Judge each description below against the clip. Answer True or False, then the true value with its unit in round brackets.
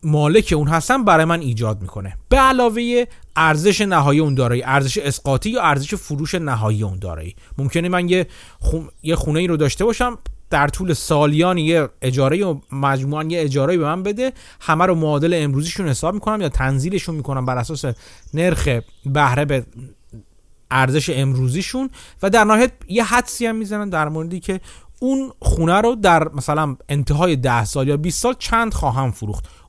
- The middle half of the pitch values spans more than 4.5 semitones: True (5.5 semitones)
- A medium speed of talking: False (170 wpm)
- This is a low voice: False (155 Hz)